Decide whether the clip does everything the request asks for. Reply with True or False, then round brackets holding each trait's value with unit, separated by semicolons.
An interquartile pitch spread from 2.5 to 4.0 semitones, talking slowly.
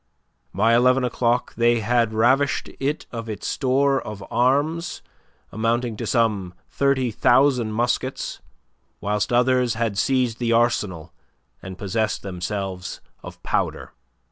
True (3.1 semitones; 120 wpm)